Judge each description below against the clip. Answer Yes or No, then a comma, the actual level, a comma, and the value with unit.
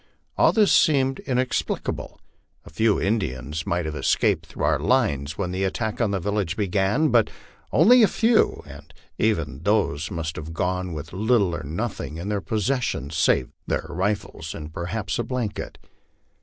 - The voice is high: No, low, 100 Hz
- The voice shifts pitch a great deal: Yes, wide, 5.9 semitones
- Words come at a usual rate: Yes, average, 160 wpm